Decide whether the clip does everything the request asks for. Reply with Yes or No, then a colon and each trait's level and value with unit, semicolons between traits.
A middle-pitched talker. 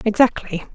No: high, 215 Hz